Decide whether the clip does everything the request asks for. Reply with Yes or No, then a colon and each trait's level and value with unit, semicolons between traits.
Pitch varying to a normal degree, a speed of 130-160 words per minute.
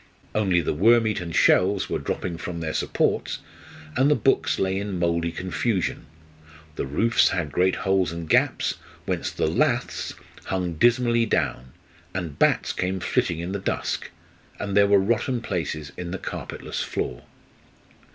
Yes: average, 4.2 semitones; average, 150 wpm